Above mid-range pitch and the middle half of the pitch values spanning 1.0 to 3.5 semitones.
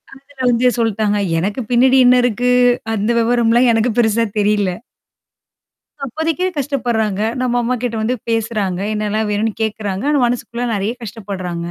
Yes: high, 225 Hz; average, 2.9 semitones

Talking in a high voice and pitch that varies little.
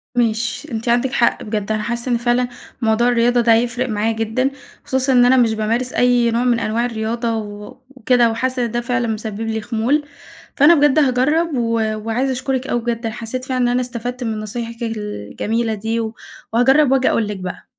Yes: high, 235 Hz; narrow, 2.1 semitones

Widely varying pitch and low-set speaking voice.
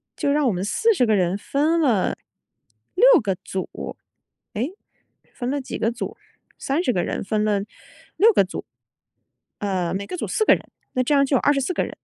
No: wide, 6.6 semitones; very high, 250 Hz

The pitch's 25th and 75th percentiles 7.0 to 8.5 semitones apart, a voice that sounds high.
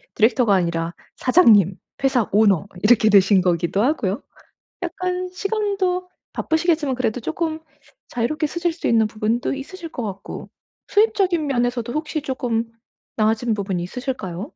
Yes: wide, 7.3 semitones; high, 245 Hz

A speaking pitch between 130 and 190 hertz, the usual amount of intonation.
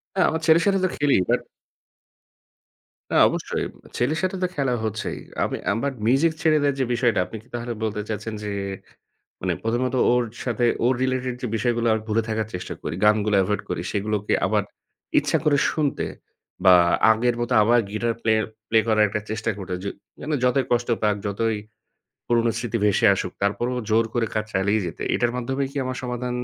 No: low, 115 Hz; average, 3.1 semitones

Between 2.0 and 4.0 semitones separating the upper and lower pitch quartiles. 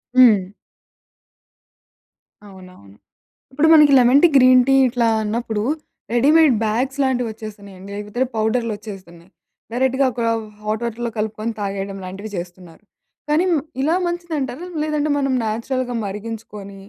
No: average, 4.6 semitones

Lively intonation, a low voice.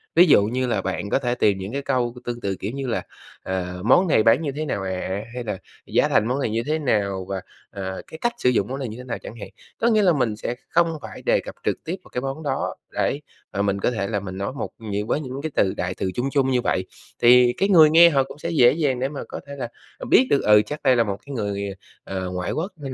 Yes: wide, 5.8 semitones; low, 125 Hz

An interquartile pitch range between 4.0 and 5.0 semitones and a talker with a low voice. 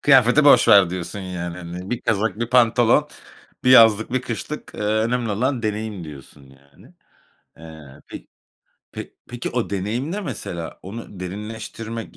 Yes: average, 4.6 semitones; low, 105 Hz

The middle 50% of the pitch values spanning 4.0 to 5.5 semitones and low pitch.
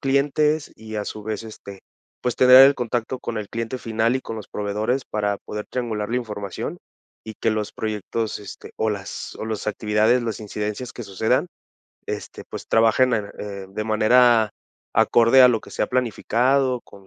No: average, 2.9 semitones; low, 110 Hz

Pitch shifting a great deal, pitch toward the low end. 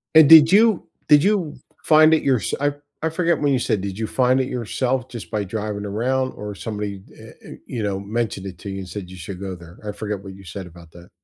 Yes: wide, 5.9 semitones; low, 105 Hz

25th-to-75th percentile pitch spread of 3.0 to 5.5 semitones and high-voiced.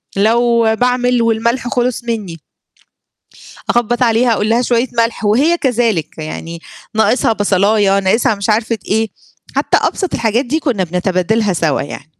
Yes: average, 3.3 semitones; high, 225 Hz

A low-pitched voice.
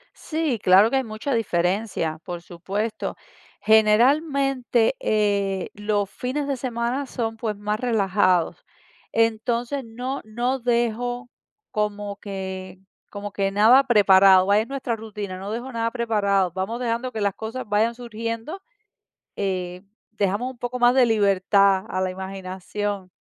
No: high, 215 Hz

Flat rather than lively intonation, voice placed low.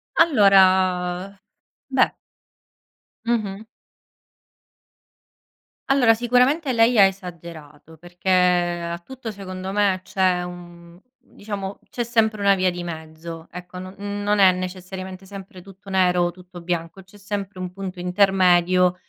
No: narrow, 2.1 semitones; medium, 185 Hz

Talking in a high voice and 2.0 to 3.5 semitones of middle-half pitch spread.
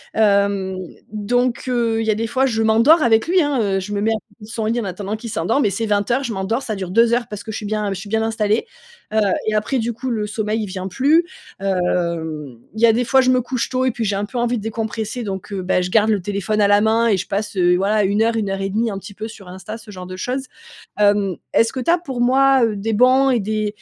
Yes: high, 220 Hz; average, 2.8 semitones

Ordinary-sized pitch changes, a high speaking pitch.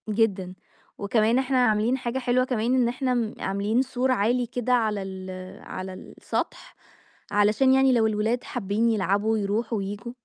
Yes: average, 3.4 semitones; high, 225 Hz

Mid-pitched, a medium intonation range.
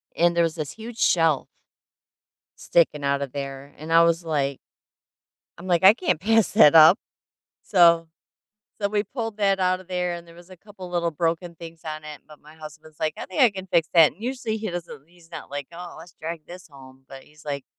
Yes: medium, 170 Hz; average, 3.2 semitones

